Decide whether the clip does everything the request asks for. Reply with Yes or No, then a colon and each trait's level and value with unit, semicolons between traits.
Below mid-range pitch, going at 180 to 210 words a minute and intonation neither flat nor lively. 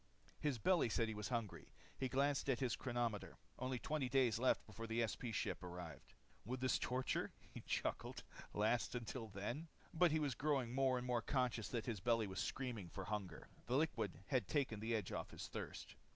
Yes: low, 120 Hz; average, 195 wpm; average, 3.3 semitones